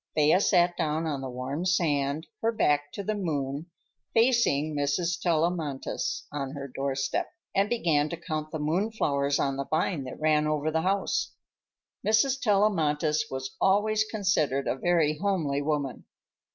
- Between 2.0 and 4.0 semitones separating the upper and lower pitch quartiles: No, average, 4.6 semitones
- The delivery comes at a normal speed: Yes, average, 150 wpm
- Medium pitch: Yes, medium, 155 Hz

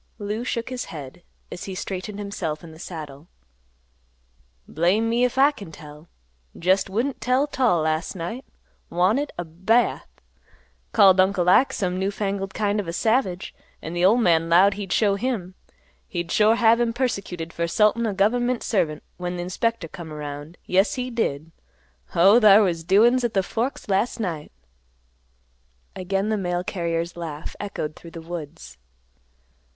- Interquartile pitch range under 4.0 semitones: No, average, 4.8 semitones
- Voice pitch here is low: No, high, 190 Hz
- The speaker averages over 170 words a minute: No, average, 165 wpm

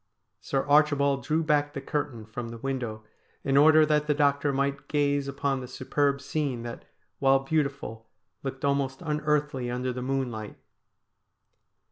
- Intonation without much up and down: Yes, narrow, 2.3 semitones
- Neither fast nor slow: Yes, average, 145 wpm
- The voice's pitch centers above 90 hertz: Yes, medium, 140 Hz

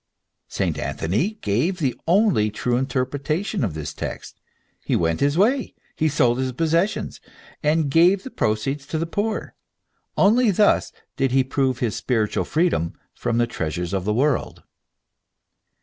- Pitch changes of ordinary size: No, wide, 6.8 semitones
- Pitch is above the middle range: No, medium, 140 Hz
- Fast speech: No, average, 150 wpm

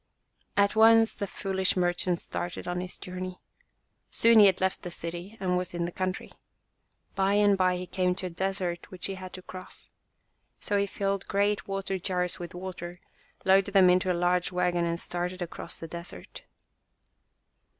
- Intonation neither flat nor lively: No, narrow, 1.6 semitones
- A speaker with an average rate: Yes, average, 175 wpm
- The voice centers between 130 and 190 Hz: Yes, medium, 185 Hz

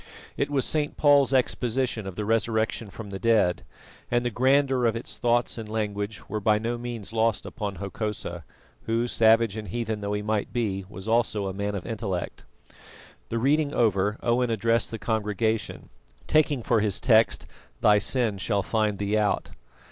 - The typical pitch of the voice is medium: No, low, 110 Hz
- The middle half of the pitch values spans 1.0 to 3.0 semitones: Yes, narrow, 2.5 semitones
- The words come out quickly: No, average, 170 wpm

